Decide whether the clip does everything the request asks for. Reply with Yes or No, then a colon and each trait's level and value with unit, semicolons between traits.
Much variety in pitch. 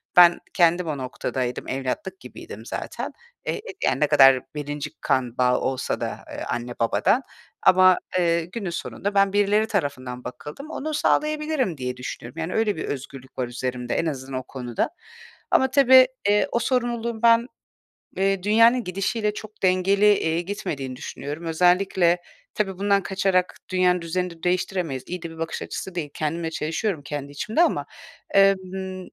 Yes: wide, 6.1 semitones